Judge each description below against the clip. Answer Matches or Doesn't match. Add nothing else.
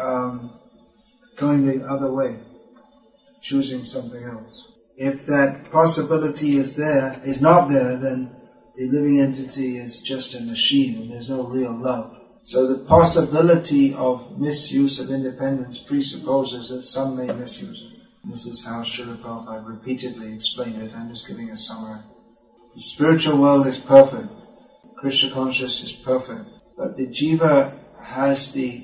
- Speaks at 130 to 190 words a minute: Matches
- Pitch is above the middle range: Doesn't match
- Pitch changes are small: Doesn't match